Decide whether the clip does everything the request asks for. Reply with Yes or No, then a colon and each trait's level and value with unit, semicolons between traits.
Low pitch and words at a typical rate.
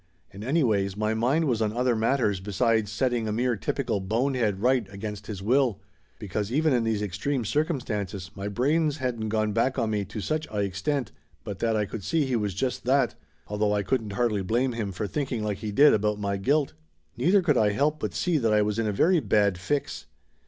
No: low, 110 Hz; fast, 215 wpm